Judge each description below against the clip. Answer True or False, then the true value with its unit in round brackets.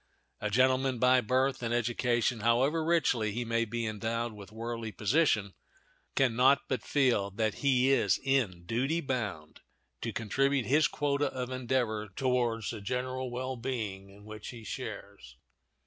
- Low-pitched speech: True (120 Hz)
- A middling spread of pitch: True (3.3 semitones)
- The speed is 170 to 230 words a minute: False (150 wpm)